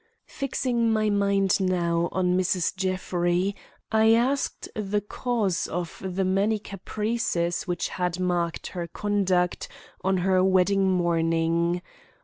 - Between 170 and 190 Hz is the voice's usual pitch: Yes, medium, 185 Hz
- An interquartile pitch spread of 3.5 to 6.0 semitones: No, average, 2.7 semitones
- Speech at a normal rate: No, slow, 120 wpm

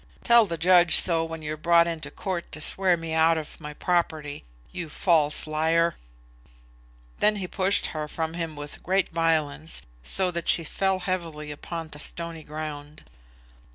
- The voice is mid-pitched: Yes, medium, 165 Hz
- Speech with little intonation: Yes, narrow, 2.2 semitones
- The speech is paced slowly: No, average, 160 wpm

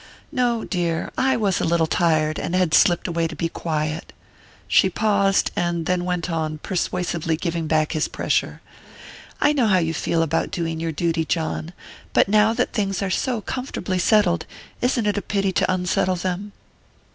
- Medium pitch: Yes, medium, 175 Hz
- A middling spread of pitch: Yes, average, 3.5 semitones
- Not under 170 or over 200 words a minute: Yes, average, 175 wpm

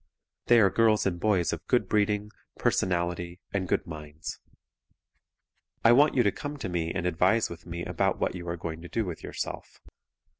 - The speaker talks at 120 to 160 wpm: No, average, 185 wpm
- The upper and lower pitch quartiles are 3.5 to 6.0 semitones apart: Yes, average, 3.8 semitones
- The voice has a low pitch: Yes, very low, 90 Hz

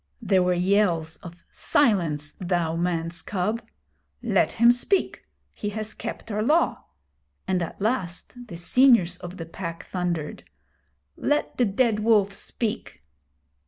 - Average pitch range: Yes, average, 4.4 semitones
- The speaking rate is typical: No, slow, 130 wpm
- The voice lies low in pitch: No, high, 190 Hz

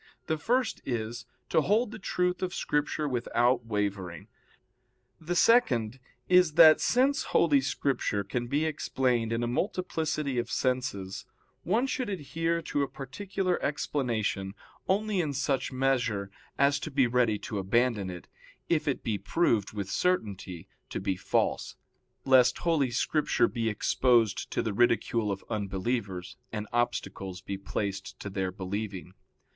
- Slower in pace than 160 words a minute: Yes, average, 140 wpm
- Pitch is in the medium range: No, low, 125 Hz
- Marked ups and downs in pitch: Yes, wide, 7.1 semitones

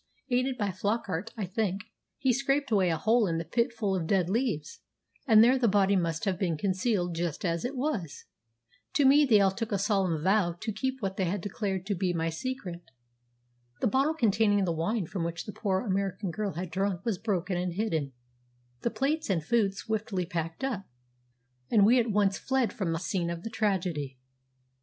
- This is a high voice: Yes, high, 195 Hz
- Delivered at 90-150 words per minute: No, average, 195 wpm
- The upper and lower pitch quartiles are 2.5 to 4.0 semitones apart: No, average, 4.4 semitones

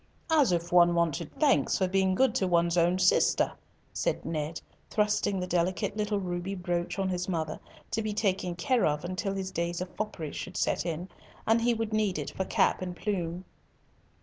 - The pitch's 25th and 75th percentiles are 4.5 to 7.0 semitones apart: No, average, 3.3 semitones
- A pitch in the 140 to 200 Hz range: Yes, medium, 185 Hz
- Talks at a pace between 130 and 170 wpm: No, average, 190 wpm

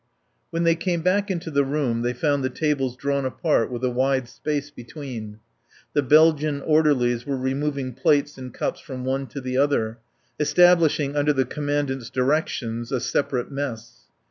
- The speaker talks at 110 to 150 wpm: No, average, 165 wpm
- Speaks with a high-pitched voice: No, medium, 140 Hz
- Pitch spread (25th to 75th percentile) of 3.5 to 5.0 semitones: No, average, 2.8 semitones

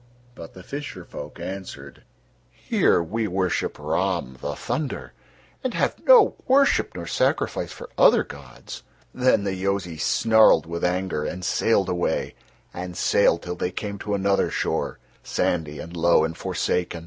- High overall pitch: No, very low, 90 Hz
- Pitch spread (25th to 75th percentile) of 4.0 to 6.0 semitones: No, average, 3.2 semitones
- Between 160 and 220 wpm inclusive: No, average, 150 wpm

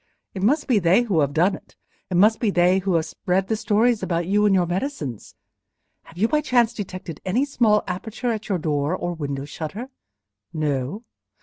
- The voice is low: No, high, 190 Hz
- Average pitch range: Yes, average, 5.0 semitones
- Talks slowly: No, average, 190 wpm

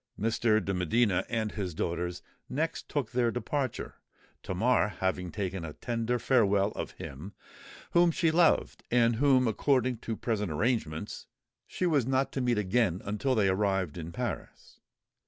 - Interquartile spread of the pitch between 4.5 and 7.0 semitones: Yes, average, 5.1 semitones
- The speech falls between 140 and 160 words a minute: Yes, average, 150 wpm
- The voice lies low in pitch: Yes, low, 110 Hz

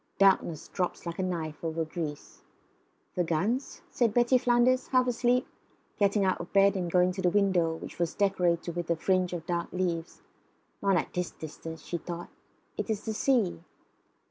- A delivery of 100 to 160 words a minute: No, average, 175 wpm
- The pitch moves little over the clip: No, average, 3.3 semitones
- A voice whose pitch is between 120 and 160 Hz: No, medium, 180 Hz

